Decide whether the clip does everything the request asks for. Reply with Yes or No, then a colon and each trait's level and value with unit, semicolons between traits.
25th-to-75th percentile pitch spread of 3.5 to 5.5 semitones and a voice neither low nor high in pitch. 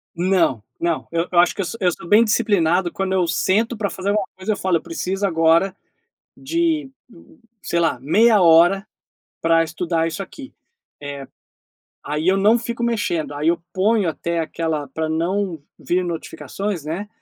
Yes: average, 3.8 semitones; medium, 180 Hz